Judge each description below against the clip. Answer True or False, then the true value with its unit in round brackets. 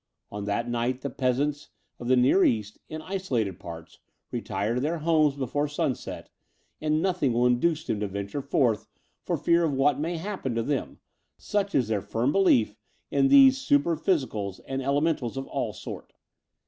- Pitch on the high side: False (135 Hz)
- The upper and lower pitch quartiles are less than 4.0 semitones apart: False (5.3 semitones)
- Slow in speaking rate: False (175 wpm)